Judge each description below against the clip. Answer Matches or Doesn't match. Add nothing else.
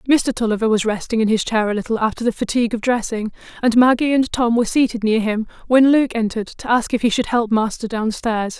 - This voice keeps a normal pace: Doesn't match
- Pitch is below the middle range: Doesn't match